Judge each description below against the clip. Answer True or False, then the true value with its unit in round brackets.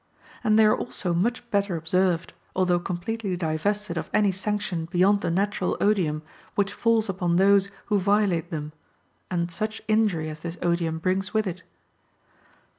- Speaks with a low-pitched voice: False (185 Hz)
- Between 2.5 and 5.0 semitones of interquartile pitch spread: True (3.4 semitones)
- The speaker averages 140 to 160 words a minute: True (155 wpm)